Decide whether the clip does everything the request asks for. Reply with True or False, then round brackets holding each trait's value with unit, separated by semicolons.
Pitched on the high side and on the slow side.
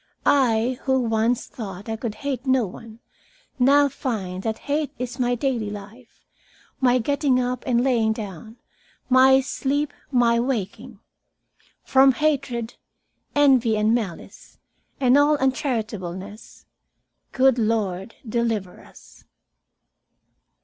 True (240 Hz; 115 wpm)